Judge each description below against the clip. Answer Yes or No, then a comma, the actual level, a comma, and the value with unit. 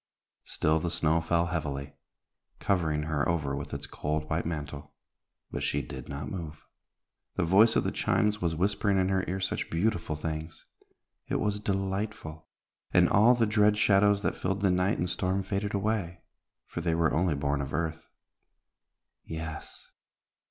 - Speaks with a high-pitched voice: No, very low, 85 Hz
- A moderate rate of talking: Yes, average, 160 wpm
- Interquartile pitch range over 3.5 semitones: Yes, average, 4.2 semitones